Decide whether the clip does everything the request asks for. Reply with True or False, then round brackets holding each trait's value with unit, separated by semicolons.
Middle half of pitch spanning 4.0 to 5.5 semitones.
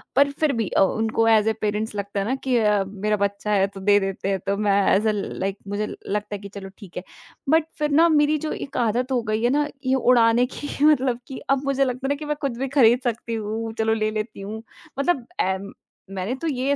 True (4.3 semitones)